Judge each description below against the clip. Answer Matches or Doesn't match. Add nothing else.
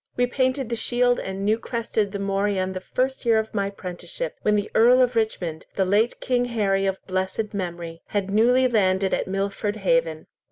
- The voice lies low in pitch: Doesn't match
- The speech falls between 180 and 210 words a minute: Matches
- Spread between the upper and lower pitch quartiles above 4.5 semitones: Doesn't match